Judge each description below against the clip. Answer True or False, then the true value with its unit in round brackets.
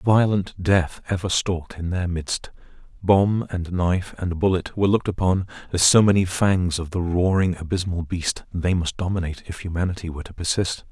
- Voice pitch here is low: True (90 Hz)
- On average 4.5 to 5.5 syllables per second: True (5.3 syllables/s)